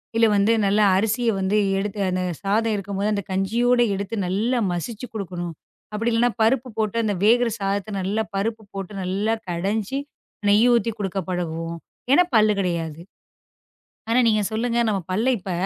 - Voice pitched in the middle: No, high, 205 Hz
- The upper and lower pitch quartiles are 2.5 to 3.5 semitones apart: Yes, average, 3.1 semitones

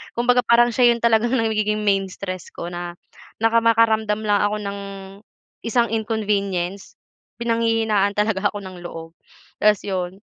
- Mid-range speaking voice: No, high, 210 Hz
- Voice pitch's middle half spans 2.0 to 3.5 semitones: Yes, narrow, 2.5 semitones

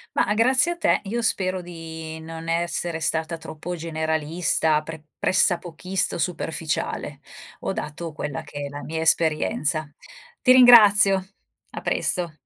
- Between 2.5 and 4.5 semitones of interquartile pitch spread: Yes, average, 2.8 semitones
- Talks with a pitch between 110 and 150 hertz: No, medium, 165 Hz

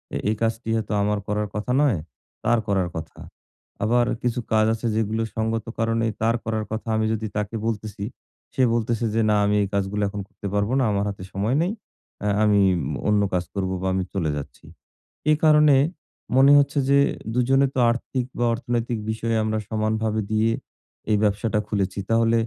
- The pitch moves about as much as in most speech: No, narrow, 2.1 semitones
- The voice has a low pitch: Yes, low, 110 Hz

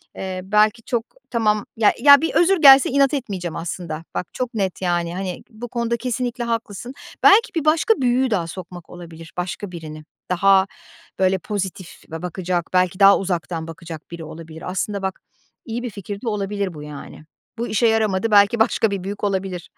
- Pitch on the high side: Yes, high, 195 Hz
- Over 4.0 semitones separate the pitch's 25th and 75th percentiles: Yes, average, 4.7 semitones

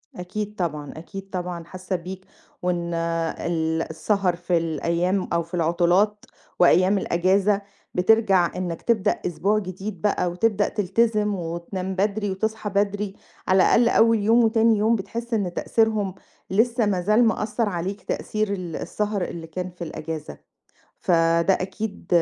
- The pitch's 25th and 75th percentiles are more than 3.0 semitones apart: Yes, average, 3.4 semitones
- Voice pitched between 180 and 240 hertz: Yes, high, 190 Hz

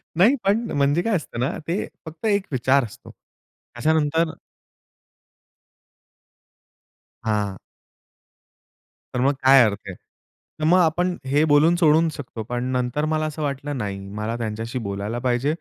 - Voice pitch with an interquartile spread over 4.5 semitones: Yes, average, 5.0 semitones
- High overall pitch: No, medium, 140 Hz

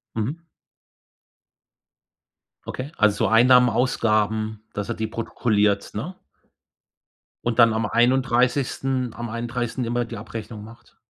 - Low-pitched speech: Yes, low, 115 Hz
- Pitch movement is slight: Yes, narrow, 2.3 semitones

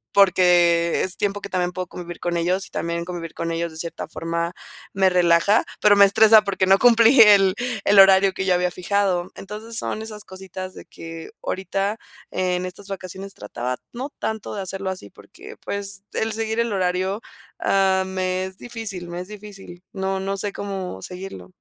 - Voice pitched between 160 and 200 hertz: Yes, high, 190 Hz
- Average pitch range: No, narrow, 2.1 semitones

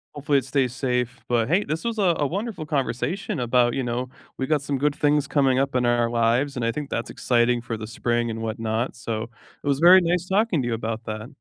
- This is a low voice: Yes, low, 130 Hz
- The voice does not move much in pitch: No, average, 4.0 semitones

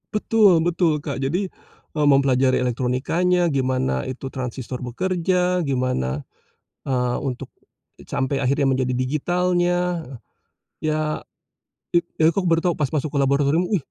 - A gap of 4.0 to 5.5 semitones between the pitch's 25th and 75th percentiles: Yes, average, 5.2 semitones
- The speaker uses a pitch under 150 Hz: Yes, medium, 140 Hz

